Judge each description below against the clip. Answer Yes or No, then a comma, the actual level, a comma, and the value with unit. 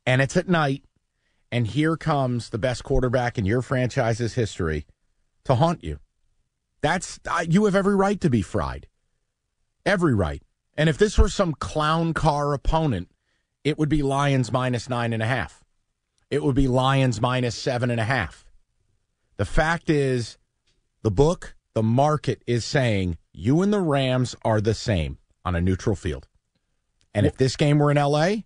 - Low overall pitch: Yes, low, 125 Hz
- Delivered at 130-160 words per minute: No, average, 170 wpm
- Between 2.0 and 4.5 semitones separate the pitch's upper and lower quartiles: No, average, 5.2 semitones